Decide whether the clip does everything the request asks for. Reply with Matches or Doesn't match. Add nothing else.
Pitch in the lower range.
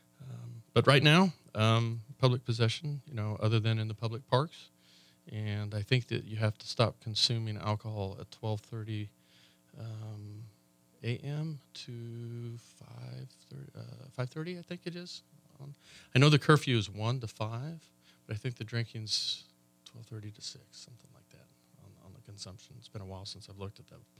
Matches